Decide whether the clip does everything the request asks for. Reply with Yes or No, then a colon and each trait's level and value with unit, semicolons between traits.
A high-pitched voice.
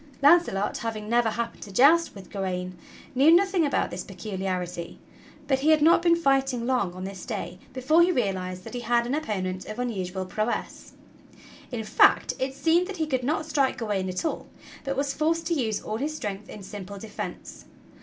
Yes: high, 235 Hz